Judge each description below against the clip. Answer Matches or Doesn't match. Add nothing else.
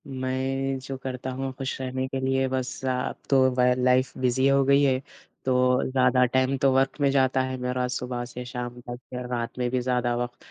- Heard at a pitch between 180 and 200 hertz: Doesn't match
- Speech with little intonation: Matches